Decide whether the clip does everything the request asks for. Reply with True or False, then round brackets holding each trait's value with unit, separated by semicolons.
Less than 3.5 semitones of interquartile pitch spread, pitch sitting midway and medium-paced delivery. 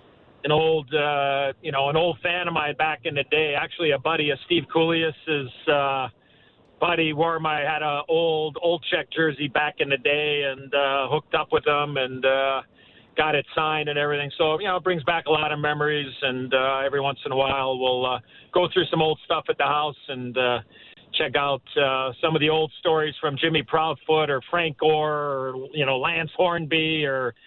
False (2.5 semitones; 150 Hz; 210 wpm)